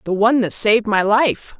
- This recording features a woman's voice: Yes, female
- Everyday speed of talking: No, fast, 225 wpm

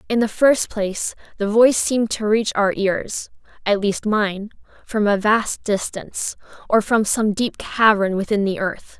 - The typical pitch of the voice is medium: No, high, 210 Hz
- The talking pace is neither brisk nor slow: Yes, average, 160 wpm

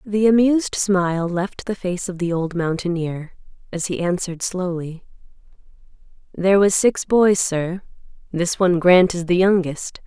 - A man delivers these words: No, female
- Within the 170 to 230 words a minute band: No, average, 150 wpm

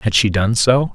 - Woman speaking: No, male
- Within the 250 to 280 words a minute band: Yes, fast, 255 wpm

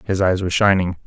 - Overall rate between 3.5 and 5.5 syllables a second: No, 6.6 syllables/s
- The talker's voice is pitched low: Yes, very low, 95 Hz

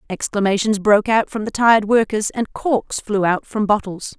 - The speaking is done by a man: No, female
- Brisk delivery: No, average, 185 wpm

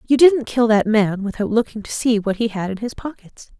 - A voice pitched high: Yes, high, 225 Hz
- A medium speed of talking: No, fast, 250 wpm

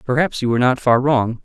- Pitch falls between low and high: No, low, 125 Hz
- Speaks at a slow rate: No, fast, 250 wpm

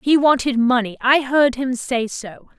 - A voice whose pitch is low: No, very high, 255 Hz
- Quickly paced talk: No, average, 185 wpm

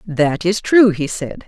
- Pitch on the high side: No, medium, 180 Hz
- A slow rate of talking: No, fast, 205 wpm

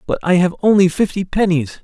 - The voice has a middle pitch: Yes, medium, 175 Hz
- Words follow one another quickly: No, average, 195 wpm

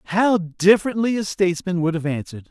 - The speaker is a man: Yes, male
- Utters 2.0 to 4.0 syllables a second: No, 6.3 syllables/s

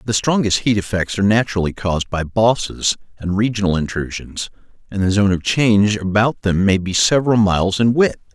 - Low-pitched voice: Yes, low, 100 Hz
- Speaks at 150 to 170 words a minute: No, average, 180 wpm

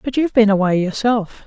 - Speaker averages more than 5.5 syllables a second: Yes, 5.8 syllables/s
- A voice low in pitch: No, high, 215 Hz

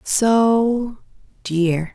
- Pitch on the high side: Yes, high, 205 Hz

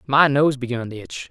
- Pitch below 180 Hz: Yes, low, 130 Hz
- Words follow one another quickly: Yes, fast, 230 wpm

